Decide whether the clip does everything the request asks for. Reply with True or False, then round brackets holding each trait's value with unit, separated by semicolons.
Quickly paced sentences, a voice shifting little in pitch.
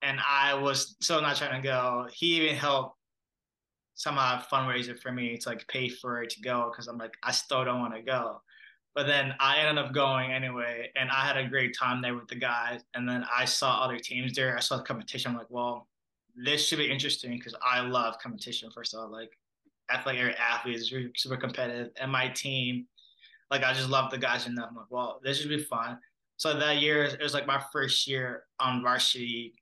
True (220 wpm; 2.2 semitones)